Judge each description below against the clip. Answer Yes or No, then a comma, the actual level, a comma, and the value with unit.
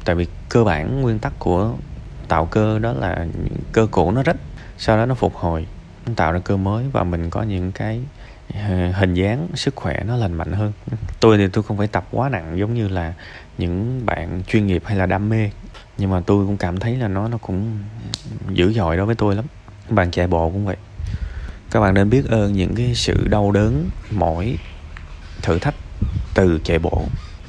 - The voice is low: Yes, low, 100 Hz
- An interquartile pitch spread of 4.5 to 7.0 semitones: No, average, 3.8 semitones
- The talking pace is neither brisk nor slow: Yes, average, 205 wpm